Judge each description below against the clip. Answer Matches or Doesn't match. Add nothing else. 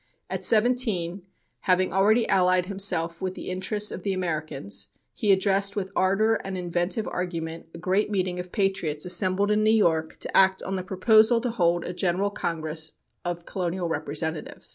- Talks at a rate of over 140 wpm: Matches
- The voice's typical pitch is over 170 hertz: Matches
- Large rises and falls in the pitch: Doesn't match